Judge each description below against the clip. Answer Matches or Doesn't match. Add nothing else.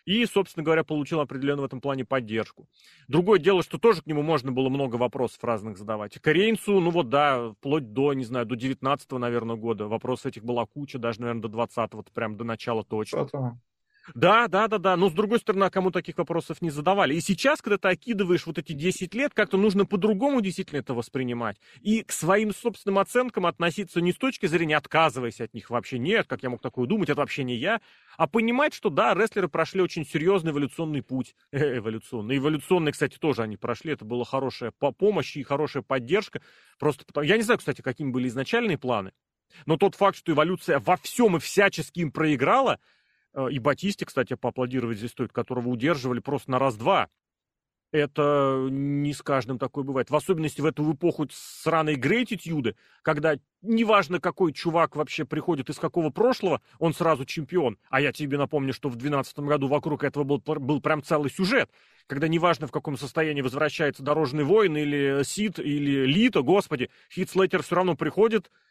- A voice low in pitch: Doesn't match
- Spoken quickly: Matches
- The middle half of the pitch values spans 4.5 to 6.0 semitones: Matches